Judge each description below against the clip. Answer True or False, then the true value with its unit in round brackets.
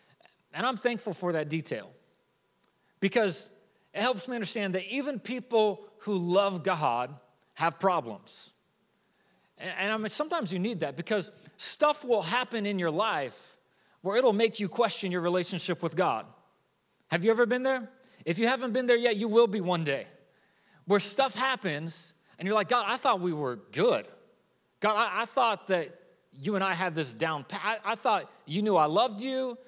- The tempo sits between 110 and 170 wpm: False (185 wpm)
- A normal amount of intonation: True (4.8 semitones)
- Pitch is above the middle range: True (205 Hz)